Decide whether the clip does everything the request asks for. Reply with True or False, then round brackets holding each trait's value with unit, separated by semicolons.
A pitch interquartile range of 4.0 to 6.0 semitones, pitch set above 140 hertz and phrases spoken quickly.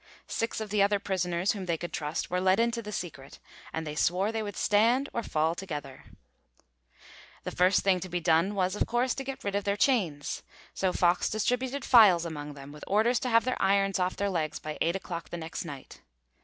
True (4.3 semitones; 190 Hz; 215 wpm)